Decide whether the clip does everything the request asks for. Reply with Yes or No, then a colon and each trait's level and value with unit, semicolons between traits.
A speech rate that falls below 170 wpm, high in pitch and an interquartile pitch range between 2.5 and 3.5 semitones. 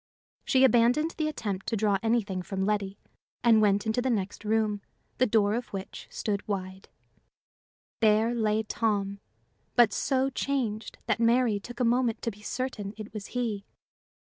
Yes: average, 160 wpm; high, 220 Hz; average, 2.9 semitones